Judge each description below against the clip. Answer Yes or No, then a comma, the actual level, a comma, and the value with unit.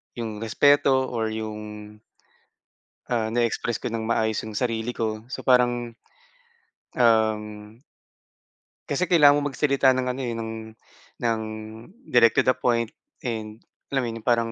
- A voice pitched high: No, low, 115 Hz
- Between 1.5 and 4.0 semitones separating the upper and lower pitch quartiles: Yes, narrow, 2.4 semitones